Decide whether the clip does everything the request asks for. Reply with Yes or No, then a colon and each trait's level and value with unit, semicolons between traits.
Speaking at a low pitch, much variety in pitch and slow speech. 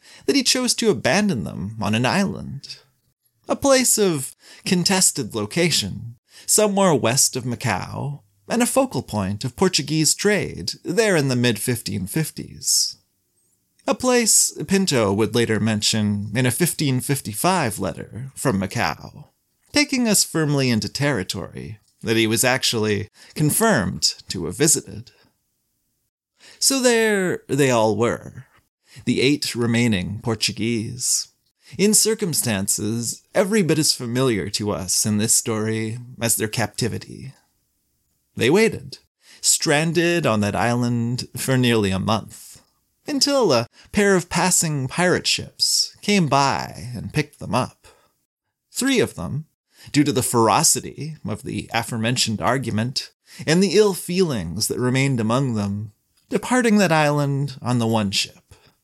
Yes: low, 130 Hz; wide, 8.0 semitones; slow, 130 wpm